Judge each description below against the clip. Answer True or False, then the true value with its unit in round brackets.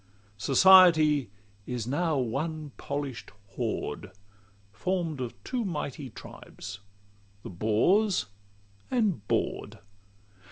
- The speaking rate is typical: False (85 wpm)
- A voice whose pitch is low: False (150 Hz)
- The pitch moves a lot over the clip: True (6.7 semitones)